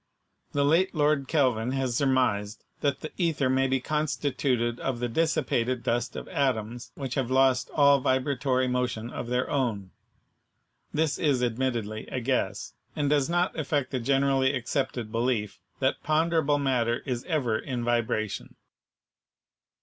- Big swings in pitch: No, average, 3.0 semitones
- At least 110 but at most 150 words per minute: Yes, average, 140 wpm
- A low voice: Yes, low, 130 Hz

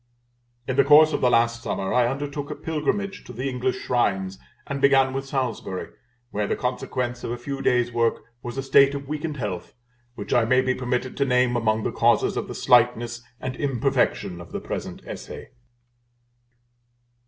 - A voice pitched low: Yes, low, 125 Hz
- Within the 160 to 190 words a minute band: Yes, average, 175 wpm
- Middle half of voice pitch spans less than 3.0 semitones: Yes, narrow, 2.6 semitones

